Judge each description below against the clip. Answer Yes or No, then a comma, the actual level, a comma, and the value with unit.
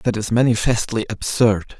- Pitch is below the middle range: Yes, low, 110 Hz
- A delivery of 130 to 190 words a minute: Yes, slow, 135 wpm